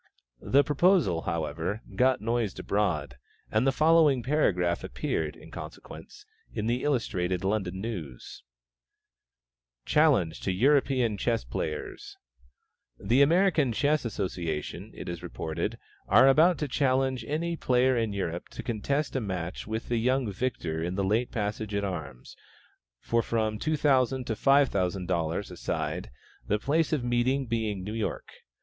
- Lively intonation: Yes, wide, 6.7 semitones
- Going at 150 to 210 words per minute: No, average, 140 wpm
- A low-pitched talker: Yes, low, 115 Hz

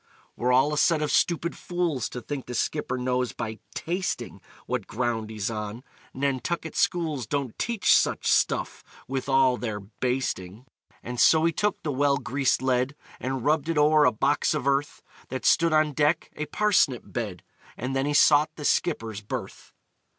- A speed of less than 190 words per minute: Yes, average, 170 wpm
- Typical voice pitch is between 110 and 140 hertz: Yes, low, 135 Hz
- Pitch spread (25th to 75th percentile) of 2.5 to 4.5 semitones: Yes, average, 3.7 semitones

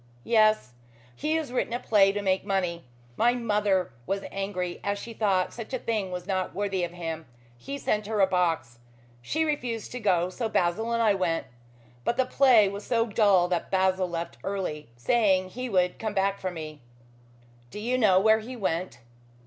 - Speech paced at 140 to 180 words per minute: No, average, 190 wpm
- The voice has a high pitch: Yes, high, 195 Hz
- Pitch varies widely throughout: No, average, 3.9 semitones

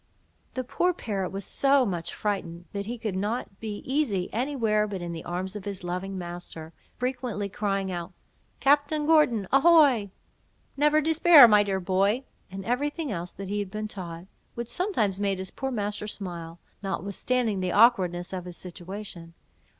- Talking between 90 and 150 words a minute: No, average, 165 wpm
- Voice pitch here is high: Yes, high, 205 Hz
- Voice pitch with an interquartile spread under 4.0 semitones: No, average, 5.2 semitones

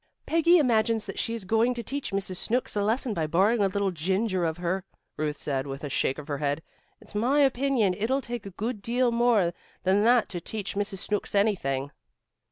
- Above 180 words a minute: Yes, average, 200 wpm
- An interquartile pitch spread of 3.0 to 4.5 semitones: No, average, 5.0 semitones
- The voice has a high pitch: Yes, high, 205 Hz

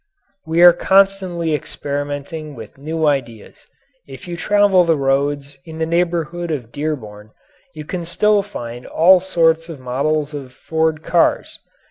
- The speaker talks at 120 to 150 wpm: Yes, slow, 135 wpm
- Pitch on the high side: No, medium, 155 Hz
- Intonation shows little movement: No, average, 3.6 semitones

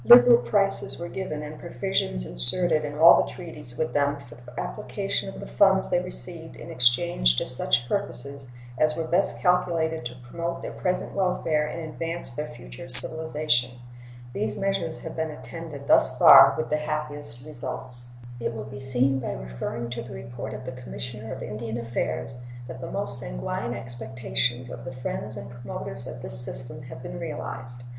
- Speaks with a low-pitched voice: Yes, low, 130 Hz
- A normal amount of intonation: Yes, average, 4.8 semitones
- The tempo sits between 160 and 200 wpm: Yes, average, 175 wpm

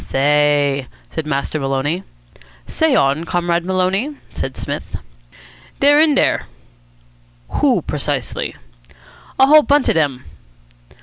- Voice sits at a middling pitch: Yes, medium, 165 Hz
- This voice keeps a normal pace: No, slow, 110 wpm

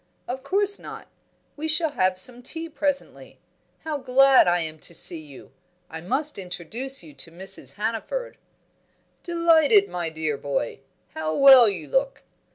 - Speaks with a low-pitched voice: No, high, 245 Hz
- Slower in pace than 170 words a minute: Yes, average, 150 wpm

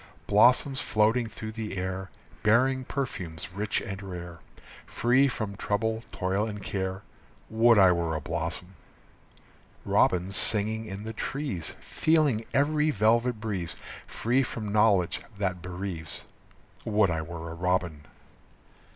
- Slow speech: Yes, slow, 125 wpm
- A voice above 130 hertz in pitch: No, low, 105 Hz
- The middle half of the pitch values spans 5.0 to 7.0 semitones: No, average, 3.8 semitones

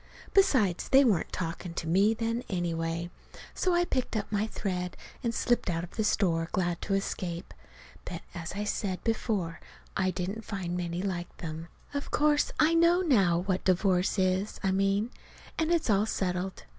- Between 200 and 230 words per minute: No, average, 170 wpm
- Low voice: No, high, 195 Hz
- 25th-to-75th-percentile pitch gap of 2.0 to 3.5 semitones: No, average, 4.2 semitones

